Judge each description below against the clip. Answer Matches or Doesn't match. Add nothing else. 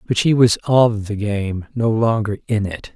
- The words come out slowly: Doesn't match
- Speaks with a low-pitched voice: Matches